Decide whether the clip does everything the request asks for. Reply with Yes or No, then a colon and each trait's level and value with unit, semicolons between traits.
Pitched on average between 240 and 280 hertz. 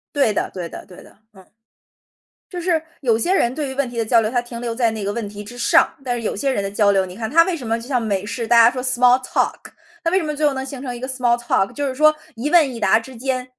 Yes: high, 245 Hz